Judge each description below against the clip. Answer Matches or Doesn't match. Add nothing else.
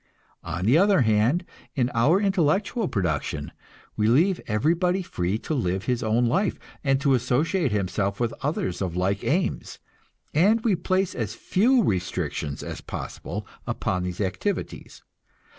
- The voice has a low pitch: Matches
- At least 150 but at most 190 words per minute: Doesn't match